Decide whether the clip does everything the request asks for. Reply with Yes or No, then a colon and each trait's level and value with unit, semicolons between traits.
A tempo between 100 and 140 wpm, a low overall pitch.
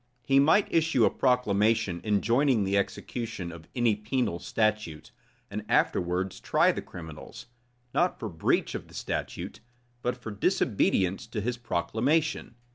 Yes: slow, 135 wpm; low, 110 Hz